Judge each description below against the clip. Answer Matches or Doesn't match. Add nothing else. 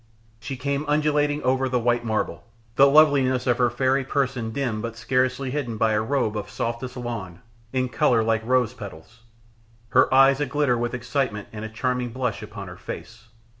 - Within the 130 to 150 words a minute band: Doesn't match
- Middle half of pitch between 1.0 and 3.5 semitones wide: Matches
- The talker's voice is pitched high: Doesn't match